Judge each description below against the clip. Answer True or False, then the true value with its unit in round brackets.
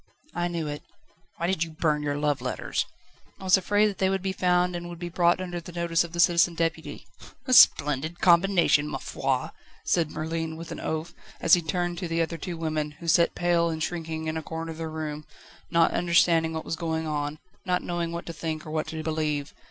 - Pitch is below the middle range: False (165 Hz)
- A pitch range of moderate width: False (1.7 semitones)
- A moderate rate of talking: False (220 wpm)